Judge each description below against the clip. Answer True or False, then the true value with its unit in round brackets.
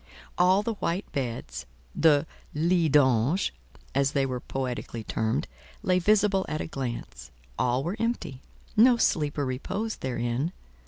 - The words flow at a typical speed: False (120 wpm)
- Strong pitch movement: True (6.6 semitones)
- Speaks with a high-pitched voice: False (145 Hz)